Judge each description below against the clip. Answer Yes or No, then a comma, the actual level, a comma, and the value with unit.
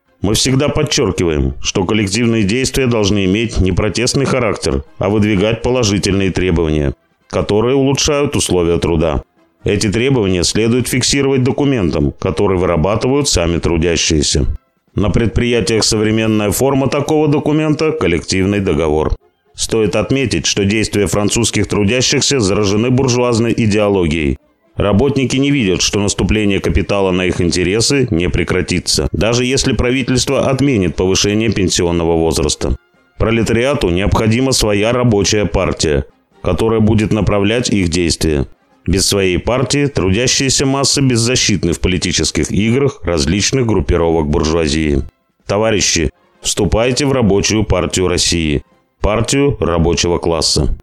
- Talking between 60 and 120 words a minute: Yes, slow, 110 wpm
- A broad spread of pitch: Yes, wide, 5.9 semitones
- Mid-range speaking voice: No, low, 105 Hz